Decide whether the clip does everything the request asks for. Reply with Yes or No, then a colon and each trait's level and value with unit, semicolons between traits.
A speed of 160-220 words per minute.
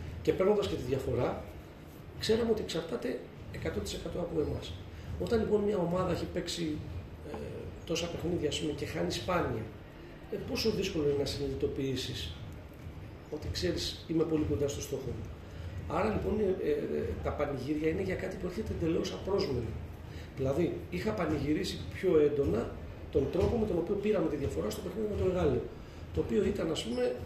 Yes: average, 165 wpm